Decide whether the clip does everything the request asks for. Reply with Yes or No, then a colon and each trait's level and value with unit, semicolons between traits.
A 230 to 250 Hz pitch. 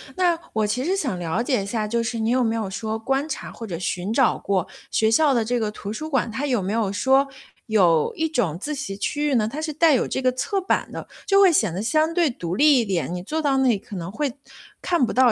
Yes: high, 235 Hz